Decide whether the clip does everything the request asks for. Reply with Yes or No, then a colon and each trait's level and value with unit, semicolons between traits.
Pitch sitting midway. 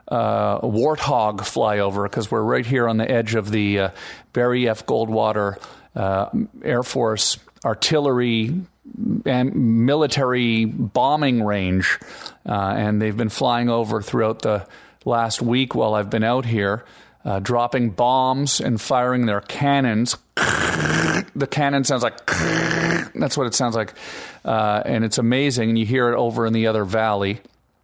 No: low, 115 Hz